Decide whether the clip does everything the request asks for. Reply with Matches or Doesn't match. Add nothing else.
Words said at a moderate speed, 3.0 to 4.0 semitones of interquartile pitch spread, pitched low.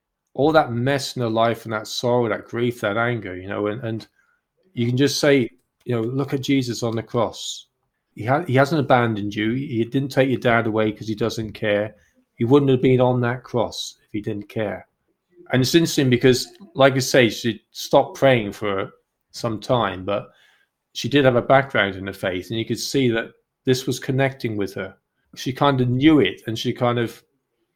Doesn't match